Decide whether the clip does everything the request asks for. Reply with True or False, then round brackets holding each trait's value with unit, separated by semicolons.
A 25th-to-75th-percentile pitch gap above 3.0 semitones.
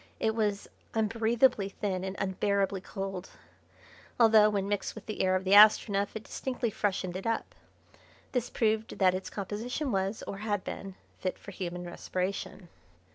False (2.4 semitones)